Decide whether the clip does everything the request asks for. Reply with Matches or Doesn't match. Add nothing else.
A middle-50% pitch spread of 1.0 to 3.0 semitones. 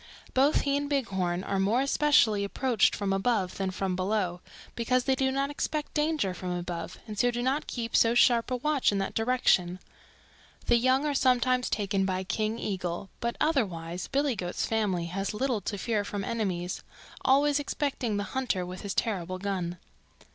Doesn't match